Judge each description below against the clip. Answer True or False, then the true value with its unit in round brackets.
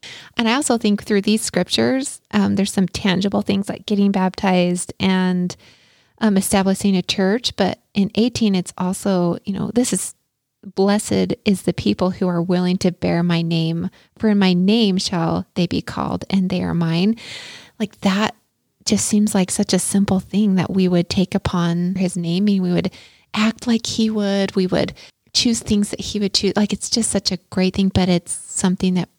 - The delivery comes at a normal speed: True (195 wpm)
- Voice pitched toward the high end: True (195 Hz)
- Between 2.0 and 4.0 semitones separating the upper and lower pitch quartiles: True (2.4 semitones)